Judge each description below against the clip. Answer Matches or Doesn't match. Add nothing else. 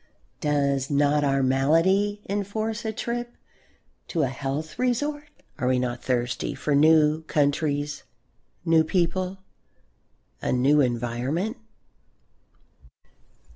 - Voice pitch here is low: Doesn't match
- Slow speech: Matches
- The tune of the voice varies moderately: Doesn't match